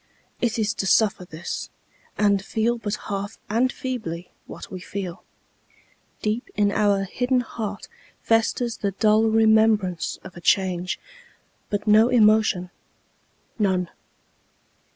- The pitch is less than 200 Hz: No, high, 210 Hz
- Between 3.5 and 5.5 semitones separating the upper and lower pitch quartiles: No, average, 2.7 semitones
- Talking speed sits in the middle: No, slow, 120 wpm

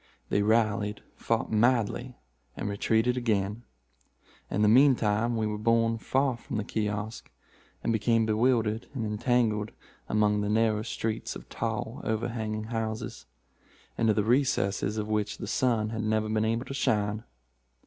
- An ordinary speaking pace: Yes, average, 150 wpm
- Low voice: Yes, low, 110 Hz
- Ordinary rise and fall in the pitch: No, narrow, 1.6 semitones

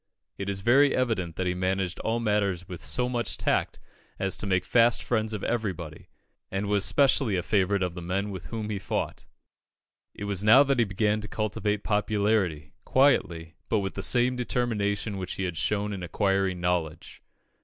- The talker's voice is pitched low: Yes, low, 100 Hz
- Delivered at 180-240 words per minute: Yes, average, 185 wpm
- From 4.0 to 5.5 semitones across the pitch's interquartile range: No, average, 3.3 semitones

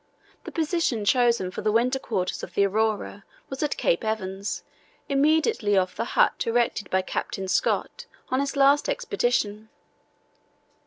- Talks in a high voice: Yes, high, 230 Hz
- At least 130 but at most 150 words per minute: Yes, average, 145 wpm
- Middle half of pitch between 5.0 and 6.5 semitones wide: Yes, wide, 5.6 semitones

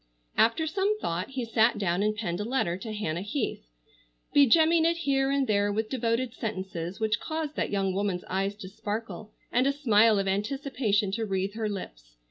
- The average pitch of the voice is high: Yes, high, 215 Hz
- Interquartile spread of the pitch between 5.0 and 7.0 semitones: Yes, wide, 5.5 semitones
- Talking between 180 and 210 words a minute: Yes, average, 185 wpm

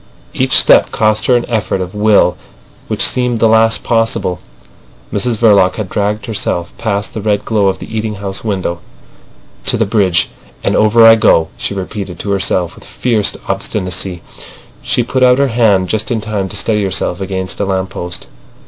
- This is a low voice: Yes, low, 105 Hz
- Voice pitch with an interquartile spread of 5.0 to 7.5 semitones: No, average, 2.9 semitones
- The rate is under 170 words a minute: No, average, 175 wpm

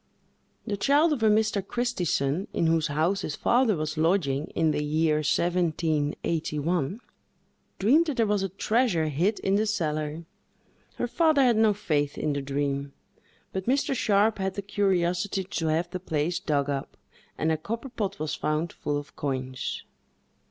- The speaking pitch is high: No, medium, 175 Hz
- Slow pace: No, average, 165 wpm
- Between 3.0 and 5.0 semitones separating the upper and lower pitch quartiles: No, wide, 5.5 semitones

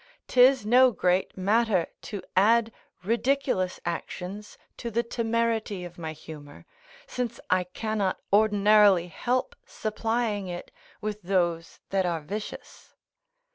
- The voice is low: No, high, 210 Hz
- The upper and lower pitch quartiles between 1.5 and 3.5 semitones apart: No, average, 4.2 semitones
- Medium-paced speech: No, slow, 115 wpm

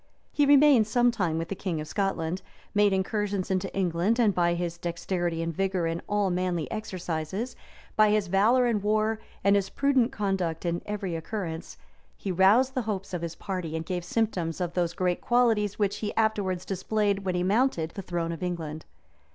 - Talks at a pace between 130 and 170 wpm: No, average, 185 wpm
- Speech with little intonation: No, average, 3.6 semitones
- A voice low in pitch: No, high, 190 Hz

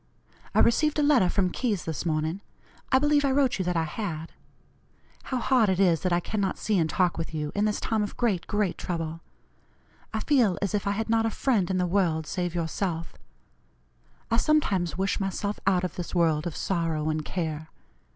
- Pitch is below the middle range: No, medium, 185 Hz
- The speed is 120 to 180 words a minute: No, average, 200 wpm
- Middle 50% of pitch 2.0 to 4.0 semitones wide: No, average, 4.6 semitones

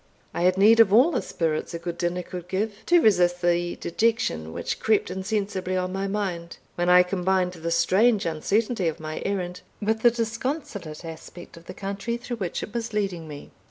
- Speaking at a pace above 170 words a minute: Yes, average, 195 wpm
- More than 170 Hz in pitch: Yes, medium, 185 Hz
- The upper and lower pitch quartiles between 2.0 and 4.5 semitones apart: Yes, average, 3.9 semitones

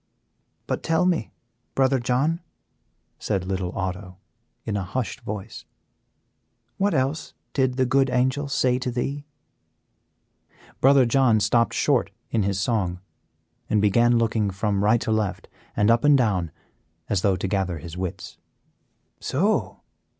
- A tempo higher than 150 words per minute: No, slow, 135 wpm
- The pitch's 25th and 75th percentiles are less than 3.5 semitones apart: No, average, 5.0 semitones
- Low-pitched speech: Yes, low, 115 Hz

